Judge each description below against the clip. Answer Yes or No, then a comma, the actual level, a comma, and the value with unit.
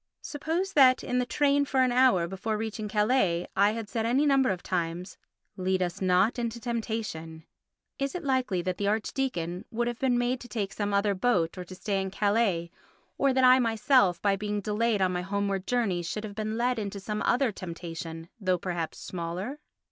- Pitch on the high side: Yes, high, 210 Hz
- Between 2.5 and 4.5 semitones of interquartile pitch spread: No, average, 5.0 semitones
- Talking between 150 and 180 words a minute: No, average, 195 wpm